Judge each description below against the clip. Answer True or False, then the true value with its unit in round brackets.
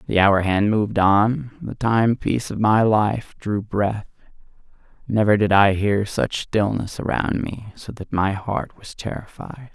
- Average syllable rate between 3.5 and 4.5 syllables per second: True (4.1 syllables/s)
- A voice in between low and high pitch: False (105 Hz)